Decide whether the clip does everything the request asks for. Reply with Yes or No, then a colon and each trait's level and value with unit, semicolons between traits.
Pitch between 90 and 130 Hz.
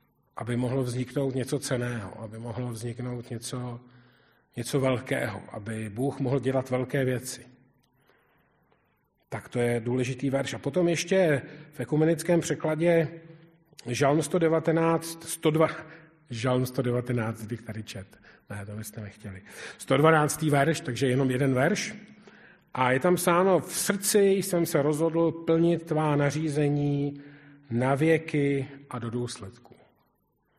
No: medium, 140 Hz